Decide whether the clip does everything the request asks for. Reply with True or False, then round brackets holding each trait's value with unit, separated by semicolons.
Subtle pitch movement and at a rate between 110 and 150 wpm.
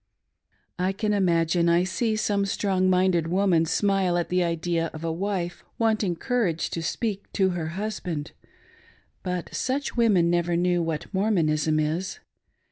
False (3.0 semitones; 145 wpm)